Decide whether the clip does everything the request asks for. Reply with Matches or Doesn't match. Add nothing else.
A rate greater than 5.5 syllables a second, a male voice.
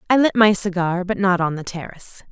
Doesn't match